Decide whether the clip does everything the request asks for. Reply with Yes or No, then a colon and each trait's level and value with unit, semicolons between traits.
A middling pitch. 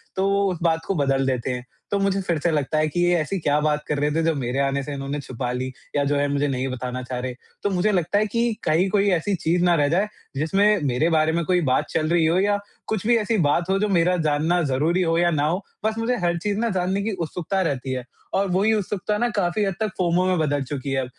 Yes: medium, 170 Hz